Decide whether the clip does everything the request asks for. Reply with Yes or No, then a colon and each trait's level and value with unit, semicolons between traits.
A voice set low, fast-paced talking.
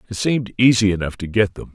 Yes: low, 105 Hz; fast, 240 wpm